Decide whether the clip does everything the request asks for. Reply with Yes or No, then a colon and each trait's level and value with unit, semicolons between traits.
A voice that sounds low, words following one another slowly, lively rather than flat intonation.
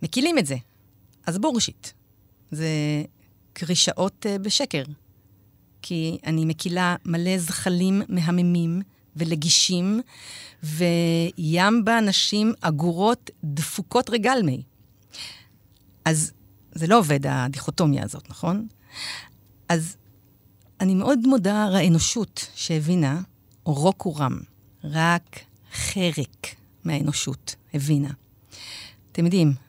No: medium, 160 Hz; slow, 85 wpm; wide, 6.5 semitones